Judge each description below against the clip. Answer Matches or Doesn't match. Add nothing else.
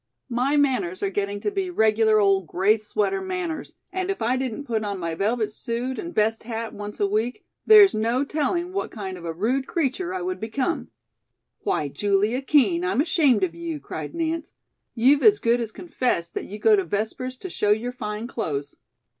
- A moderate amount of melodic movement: Doesn't match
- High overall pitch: Matches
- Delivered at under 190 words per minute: Doesn't match